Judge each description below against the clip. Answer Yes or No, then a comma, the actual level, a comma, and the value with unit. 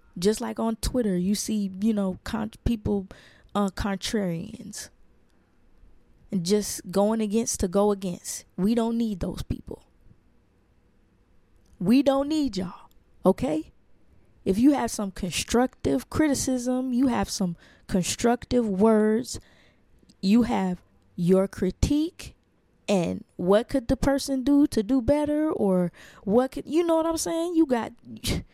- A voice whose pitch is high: Yes, high, 215 Hz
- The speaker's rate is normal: No, slow, 130 wpm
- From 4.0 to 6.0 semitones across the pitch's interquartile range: Yes, average, 5.3 semitones